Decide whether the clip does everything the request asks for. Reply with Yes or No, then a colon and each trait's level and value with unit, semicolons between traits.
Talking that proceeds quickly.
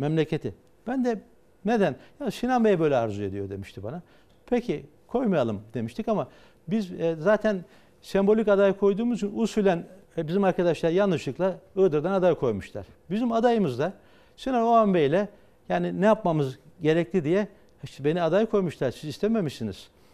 Yes: fast, 145 wpm